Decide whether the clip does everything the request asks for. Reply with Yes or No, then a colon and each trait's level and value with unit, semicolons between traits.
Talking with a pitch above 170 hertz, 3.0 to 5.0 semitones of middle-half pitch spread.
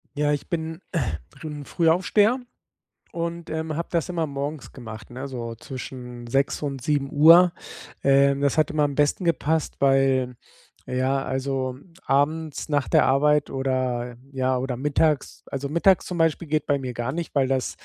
No: medium, 140 Hz; average, 3.4 semitones